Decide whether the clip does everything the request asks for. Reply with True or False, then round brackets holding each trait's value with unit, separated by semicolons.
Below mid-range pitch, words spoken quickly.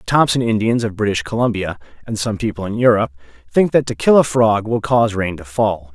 True (110 Hz; 220 wpm)